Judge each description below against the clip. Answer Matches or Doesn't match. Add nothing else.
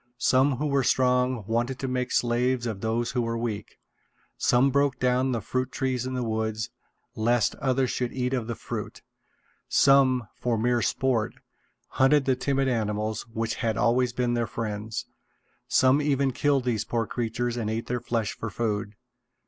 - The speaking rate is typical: Matches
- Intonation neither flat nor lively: Doesn't match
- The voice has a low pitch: Matches